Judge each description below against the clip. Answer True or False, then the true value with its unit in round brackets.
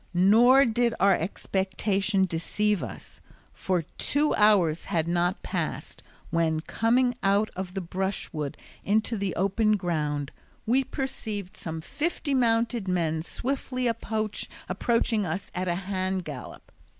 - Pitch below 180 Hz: False (195 Hz)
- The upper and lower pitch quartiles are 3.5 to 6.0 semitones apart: True (4.5 semitones)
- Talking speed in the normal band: False (125 wpm)